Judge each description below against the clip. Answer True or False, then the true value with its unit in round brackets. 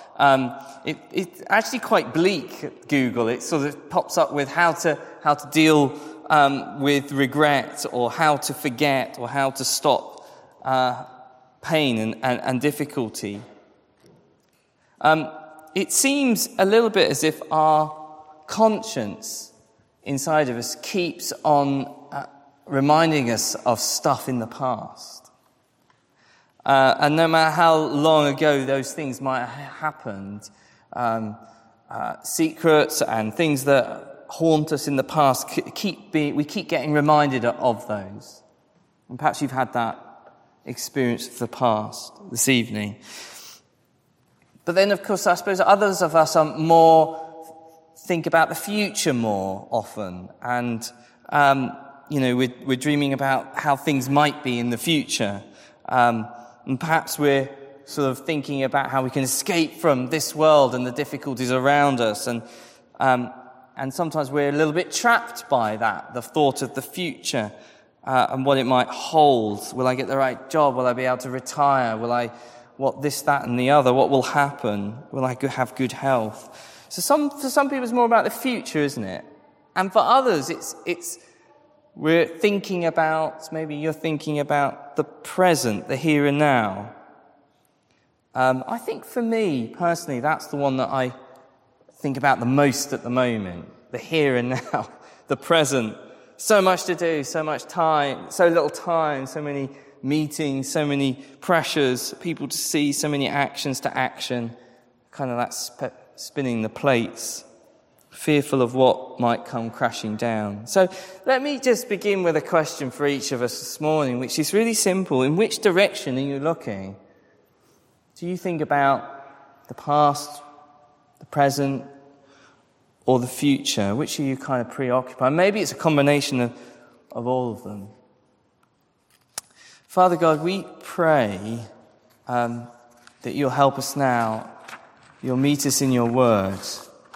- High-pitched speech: False (140 Hz)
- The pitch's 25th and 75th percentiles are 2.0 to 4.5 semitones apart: True (3.7 semitones)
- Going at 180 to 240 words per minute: False (155 wpm)